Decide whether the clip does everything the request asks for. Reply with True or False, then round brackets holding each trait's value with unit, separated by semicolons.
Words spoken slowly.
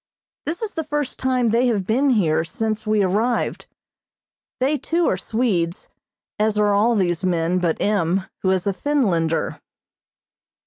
False (150 wpm)